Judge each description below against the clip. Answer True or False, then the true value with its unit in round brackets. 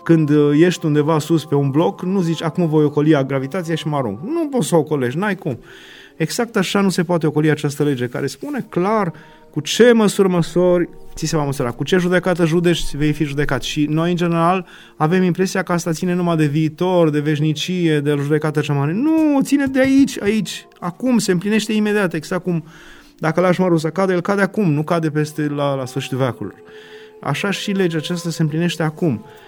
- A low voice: False (170 Hz)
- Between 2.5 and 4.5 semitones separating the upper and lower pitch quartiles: True (3.7 semitones)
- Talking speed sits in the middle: False (205 wpm)